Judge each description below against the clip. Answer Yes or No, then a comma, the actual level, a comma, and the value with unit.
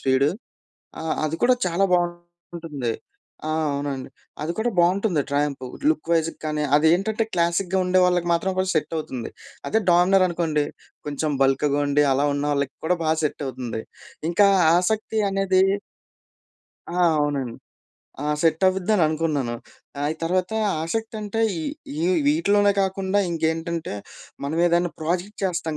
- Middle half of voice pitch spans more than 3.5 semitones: Yes, average, 4.0 semitones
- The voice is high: No, medium, 170 Hz